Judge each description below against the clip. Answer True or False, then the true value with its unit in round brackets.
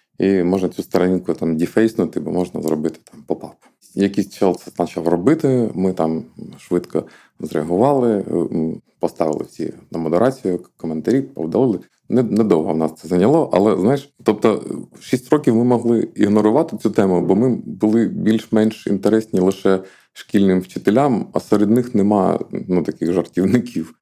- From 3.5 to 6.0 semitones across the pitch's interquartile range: True (3.9 semitones)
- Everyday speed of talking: True (140 wpm)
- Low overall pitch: True (95 Hz)